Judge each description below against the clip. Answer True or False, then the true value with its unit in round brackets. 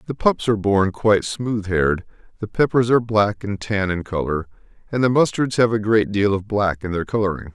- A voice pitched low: True (105 Hz)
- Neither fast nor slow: False (215 wpm)